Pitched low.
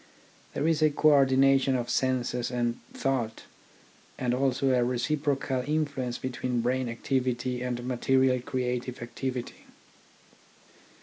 Yes: low, 130 Hz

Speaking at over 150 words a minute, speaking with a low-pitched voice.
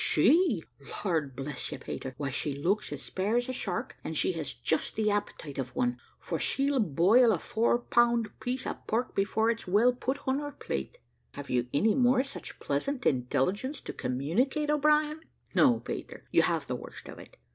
No: average, 190 wpm; high, 210 Hz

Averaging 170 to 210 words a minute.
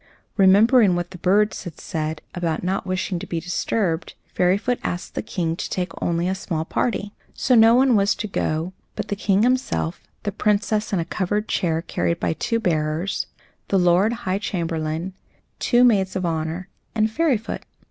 Yes: average, 175 wpm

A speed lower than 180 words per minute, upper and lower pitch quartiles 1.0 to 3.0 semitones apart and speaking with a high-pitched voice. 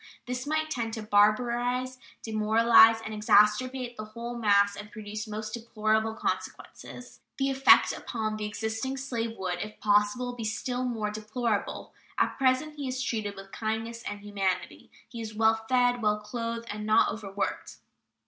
Yes: average, 155 wpm; narrow, 2.6 semitones; high, 220 Hz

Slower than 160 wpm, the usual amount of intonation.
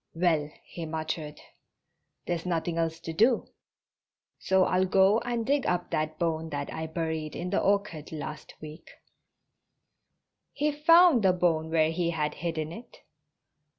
Yes: average, 145 wpm; average, 3.3 semitones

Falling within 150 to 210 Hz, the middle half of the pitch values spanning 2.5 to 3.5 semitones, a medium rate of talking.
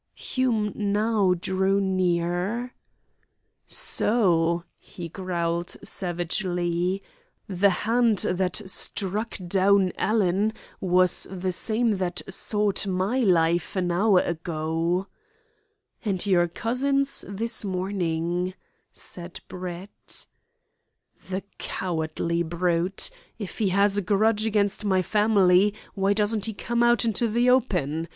No: high, 190 Hz; average, 3.2 semitones; slow, 105 wpm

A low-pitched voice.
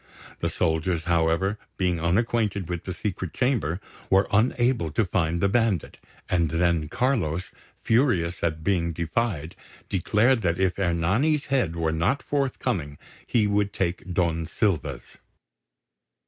Yes: very low, 90 Hz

